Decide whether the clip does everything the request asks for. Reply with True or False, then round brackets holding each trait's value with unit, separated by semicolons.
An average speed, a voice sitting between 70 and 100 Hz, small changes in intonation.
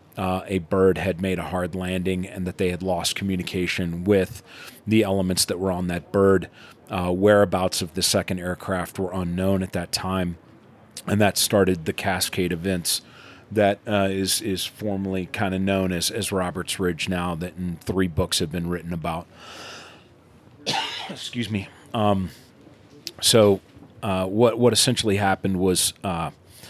True (160 wpm; 95 Hz; 1.8 semitones)